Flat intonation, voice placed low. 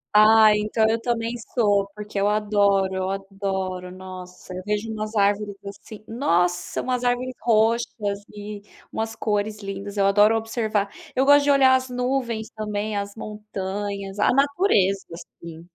No: narrow, 2.2 semitones; high, 210 Hz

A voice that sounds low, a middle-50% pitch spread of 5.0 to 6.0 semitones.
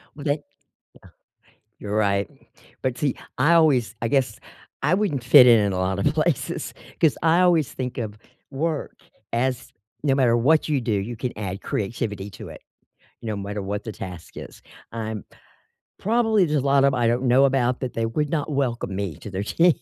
Yes: low, 125 Hz; wide, 5.6 semitones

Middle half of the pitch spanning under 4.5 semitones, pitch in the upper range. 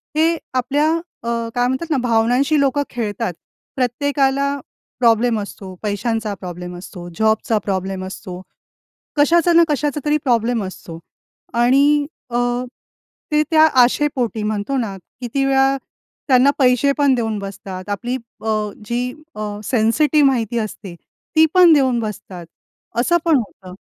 No: average, 5.1 semitones; high, 240 Hz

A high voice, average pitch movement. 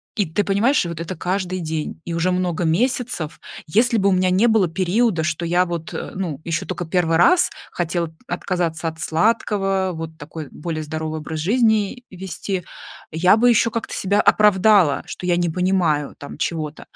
No: medium, 180 Hz; average, 3.7 semitones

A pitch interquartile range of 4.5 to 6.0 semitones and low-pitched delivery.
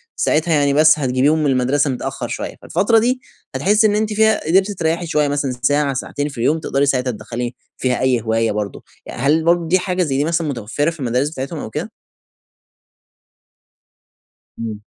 No: average, 4.8 semitones; medium, 145 Hz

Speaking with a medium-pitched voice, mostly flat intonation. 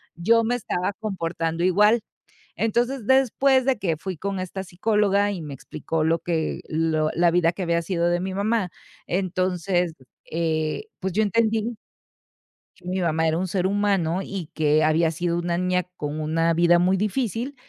No: medium, 180 Hz; average, 3.7 semitones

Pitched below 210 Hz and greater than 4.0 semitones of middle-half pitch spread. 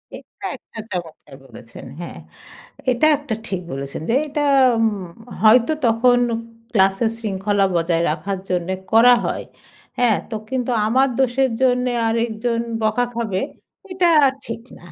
No: high, 225 Hz; average, 4.4 semitones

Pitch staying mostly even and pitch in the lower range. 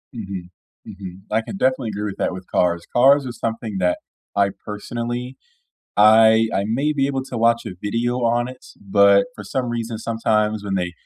No: average, 3.2 semitones; low, 110 Hz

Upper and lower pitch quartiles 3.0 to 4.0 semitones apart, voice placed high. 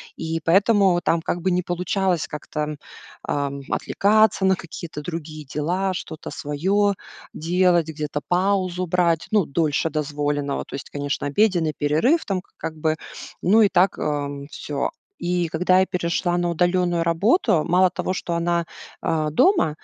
No: average, 3.4 semitones; medium, 170 Hz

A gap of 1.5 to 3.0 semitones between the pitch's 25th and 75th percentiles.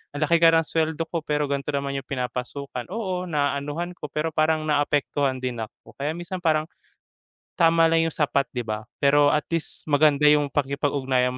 Yes: narrow, 2.6 semitones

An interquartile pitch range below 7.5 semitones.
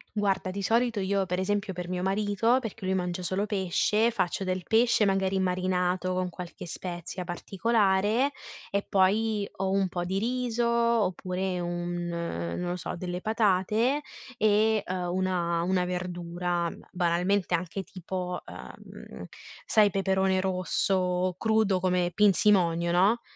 Yes: narrow, 2.4 semitones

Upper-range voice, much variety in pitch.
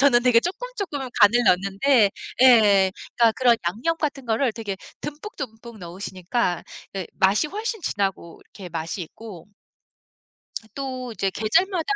Yes: high, 230 Hz; wide, 6.0 semitones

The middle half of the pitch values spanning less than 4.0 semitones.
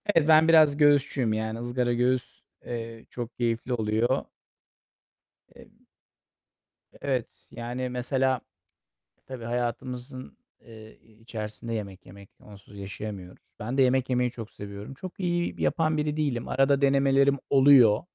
Yes: average, 3.4 semitones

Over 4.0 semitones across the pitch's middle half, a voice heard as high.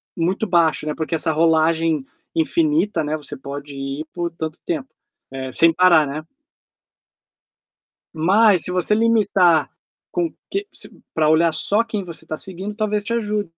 No: average, 5.1 semitones; medium, 170 Hz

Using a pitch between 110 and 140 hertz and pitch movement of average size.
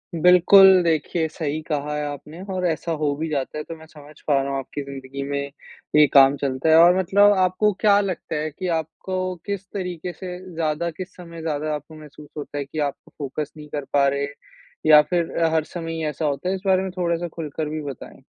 No: medium, 155 Hz; average, 3.5 semitones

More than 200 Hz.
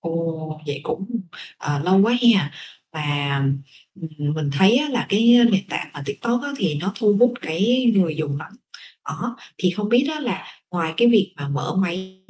No: medium, 185 Hz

